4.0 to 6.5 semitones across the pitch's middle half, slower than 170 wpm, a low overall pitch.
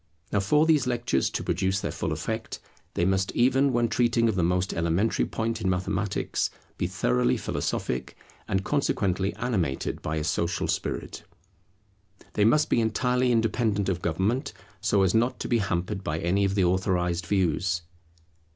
Yes: average, 4.7 semitones; average, 160 wpm; low, 100 Hz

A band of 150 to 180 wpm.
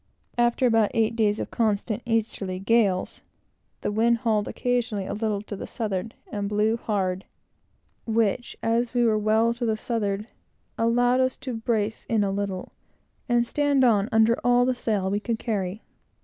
Yes: average, 165 wpm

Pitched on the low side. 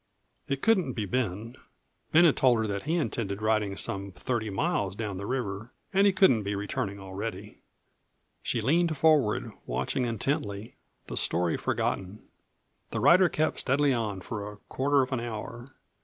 Yes: low, 115 Hz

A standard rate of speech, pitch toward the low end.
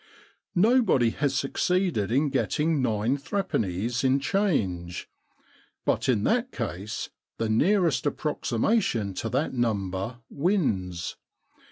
No: slow, 110 wpm; low, 130 Hz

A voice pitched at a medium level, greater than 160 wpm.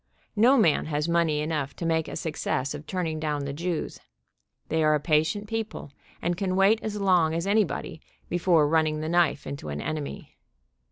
Yes: medium, 160 Hz; average, 185 wpm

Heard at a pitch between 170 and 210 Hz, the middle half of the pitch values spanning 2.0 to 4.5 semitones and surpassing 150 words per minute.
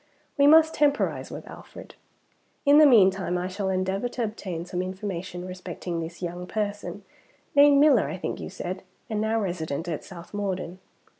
Yes: high, 190 Hz; average, 3.6 semitones; average, 165 wpm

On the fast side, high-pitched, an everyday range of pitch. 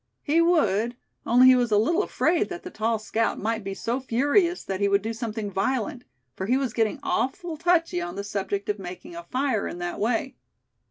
No: fast, 210 wpm; high, 230 Hz; wide, 6.0 semitones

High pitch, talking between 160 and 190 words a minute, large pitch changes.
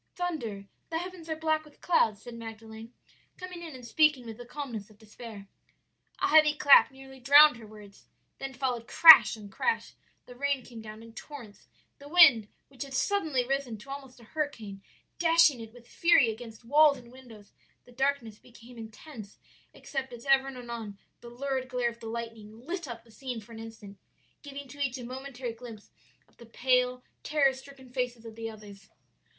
No: very high, 250 Hz; average, 185 wpm; average, 3.9 semitones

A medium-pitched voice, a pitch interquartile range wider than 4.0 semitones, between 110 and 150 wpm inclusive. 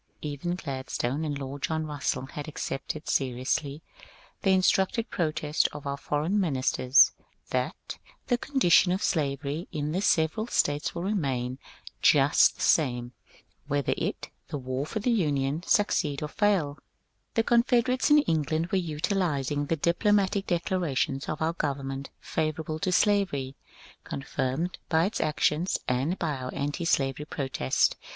Yes: medium, 155 Hz; average, 4.6 semitones; average, 140 wpm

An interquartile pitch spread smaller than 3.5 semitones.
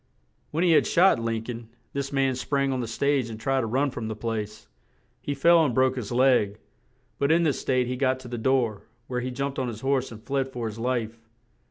Yes: average, 3.0 semitones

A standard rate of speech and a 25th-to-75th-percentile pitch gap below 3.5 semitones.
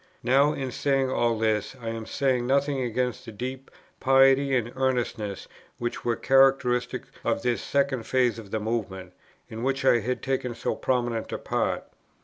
Yes: average, 165 wpm; average, 2.7 semitones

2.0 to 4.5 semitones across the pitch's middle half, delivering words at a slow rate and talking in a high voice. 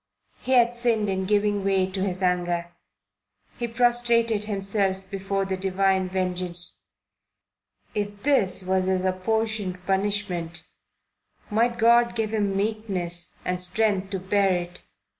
Yes: average, 2.8 semitones; slow, 125 wpm; high, 195 Hz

